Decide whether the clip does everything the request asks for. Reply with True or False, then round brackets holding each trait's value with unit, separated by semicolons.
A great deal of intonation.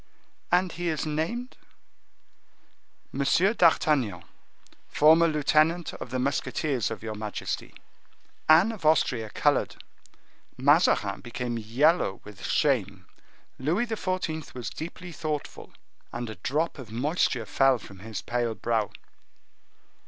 True (6.3 semitones)